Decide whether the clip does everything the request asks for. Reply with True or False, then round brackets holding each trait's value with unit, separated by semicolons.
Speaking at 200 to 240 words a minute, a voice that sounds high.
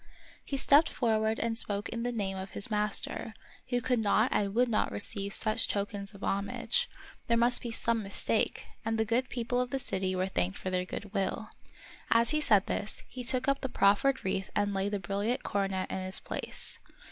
True (205 wpm; 215 Hz)